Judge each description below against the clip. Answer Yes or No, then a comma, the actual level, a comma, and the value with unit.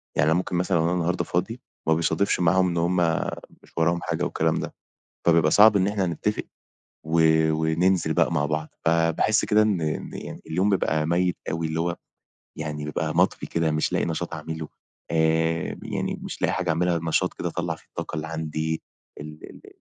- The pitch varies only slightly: Yes, narrow, 2.0 semitones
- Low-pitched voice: Yes, very low, 80 Hz